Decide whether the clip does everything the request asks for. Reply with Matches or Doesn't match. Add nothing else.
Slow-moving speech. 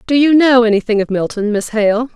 Doesn't match